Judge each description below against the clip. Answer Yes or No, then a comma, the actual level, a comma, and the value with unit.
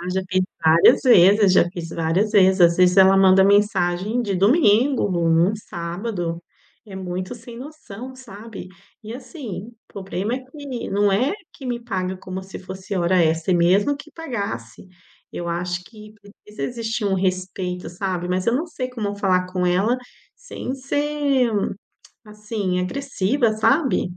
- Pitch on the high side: Yes, high, 200 Hz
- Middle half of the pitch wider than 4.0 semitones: Yes, average, 4.6 semitones